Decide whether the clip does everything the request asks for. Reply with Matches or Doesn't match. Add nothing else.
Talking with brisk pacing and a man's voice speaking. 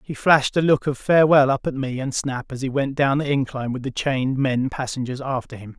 Matches